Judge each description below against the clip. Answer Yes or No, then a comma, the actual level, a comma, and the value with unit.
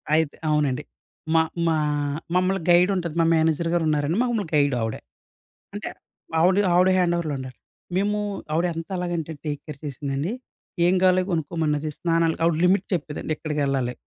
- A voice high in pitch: No, medium, 165 Hz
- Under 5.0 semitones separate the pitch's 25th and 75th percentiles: Yes, average, 3.3 semitones